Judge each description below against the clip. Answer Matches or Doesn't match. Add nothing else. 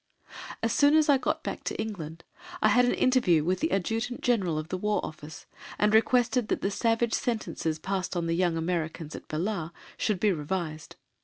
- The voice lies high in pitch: Matches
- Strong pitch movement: Matches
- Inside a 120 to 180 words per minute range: Doesn't match